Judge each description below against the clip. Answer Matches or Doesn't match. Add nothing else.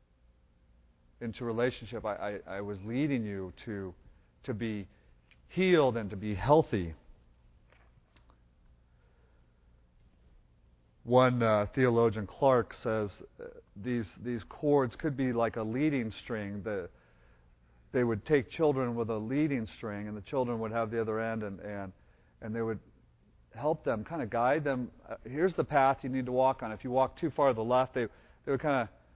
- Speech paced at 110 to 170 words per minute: Matches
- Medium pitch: Doesn't match